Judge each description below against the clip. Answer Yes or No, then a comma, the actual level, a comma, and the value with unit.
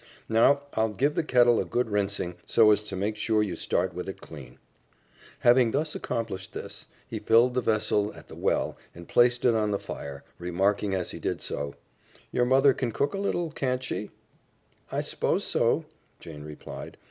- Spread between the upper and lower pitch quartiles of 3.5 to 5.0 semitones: Yes, average, 4.4 semitones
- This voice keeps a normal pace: Yes, average, 180 wpm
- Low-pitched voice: Yes, low, 110 Hz